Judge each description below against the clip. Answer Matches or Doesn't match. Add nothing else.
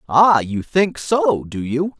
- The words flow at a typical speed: Matches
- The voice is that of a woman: Doesn't match